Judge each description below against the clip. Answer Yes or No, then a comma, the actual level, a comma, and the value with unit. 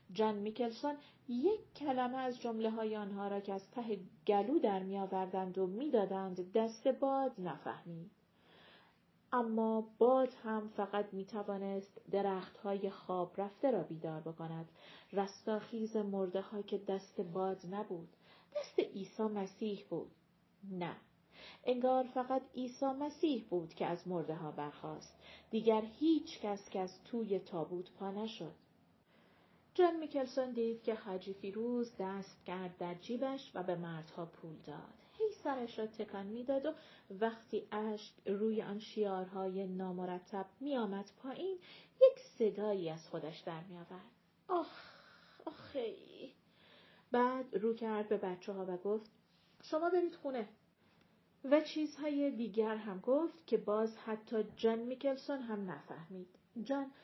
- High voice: Yes, high, 210 Hz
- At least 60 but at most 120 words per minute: No, average, 130 wpm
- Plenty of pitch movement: No, average, 4.8 semitones